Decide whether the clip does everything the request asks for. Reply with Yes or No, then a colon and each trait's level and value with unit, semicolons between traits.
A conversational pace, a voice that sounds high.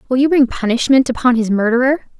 Yes: average, 190 wpm; very high, 250 Hz